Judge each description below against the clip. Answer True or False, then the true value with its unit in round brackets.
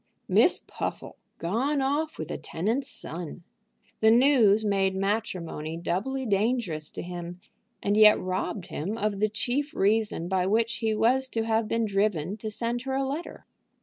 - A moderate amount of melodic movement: True (4.2 semitones)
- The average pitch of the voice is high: True (215 Hz)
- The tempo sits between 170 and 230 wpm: False (160 wpm)